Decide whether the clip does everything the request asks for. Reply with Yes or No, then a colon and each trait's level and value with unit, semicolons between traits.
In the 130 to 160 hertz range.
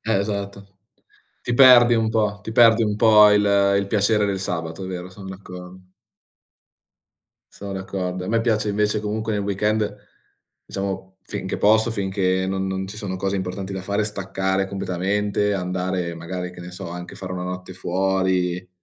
No: very low, 95 Hz